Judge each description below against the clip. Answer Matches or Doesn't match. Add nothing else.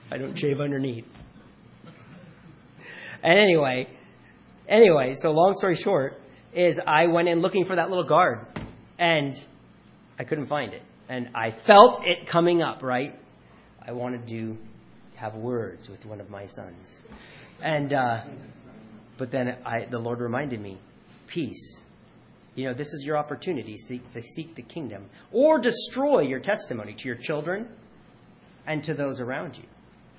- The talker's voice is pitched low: Matches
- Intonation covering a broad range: Matches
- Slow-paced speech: Doesn't match